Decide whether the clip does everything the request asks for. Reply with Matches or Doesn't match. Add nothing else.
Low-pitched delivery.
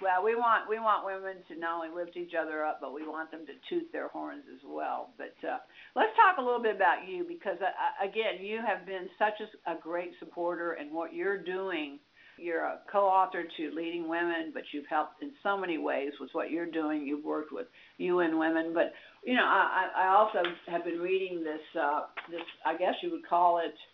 Doesn't match